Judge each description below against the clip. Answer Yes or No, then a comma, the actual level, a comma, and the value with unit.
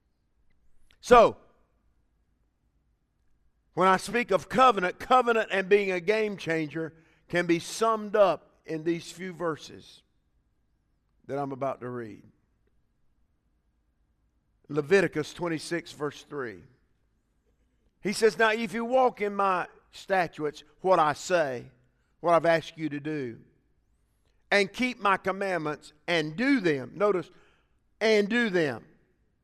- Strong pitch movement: Yes, wide, 6.6 semitones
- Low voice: No, medium, 165 Hz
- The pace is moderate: No, slow, 120 wpm